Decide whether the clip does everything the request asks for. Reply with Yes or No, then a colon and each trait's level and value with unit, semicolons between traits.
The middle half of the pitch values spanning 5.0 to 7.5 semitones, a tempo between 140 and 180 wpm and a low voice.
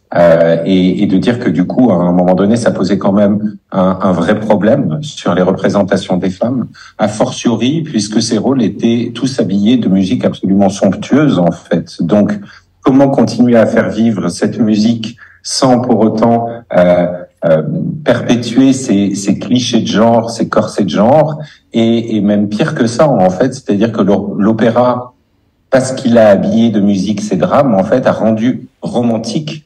No: average, 3.8 semitones; average, 175 wpm; low, 115 Hz